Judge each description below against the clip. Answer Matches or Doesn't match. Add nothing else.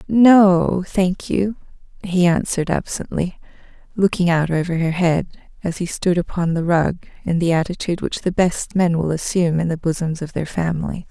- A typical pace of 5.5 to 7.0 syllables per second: Doesn't match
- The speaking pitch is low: Doesn't match